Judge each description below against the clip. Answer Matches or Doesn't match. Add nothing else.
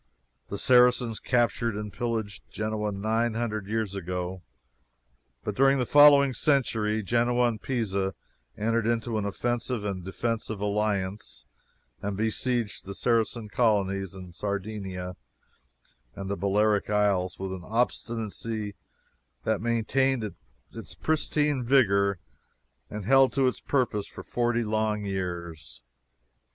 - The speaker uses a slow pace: Matches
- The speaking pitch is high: Doesn't match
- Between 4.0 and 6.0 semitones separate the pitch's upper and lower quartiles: Doesn't match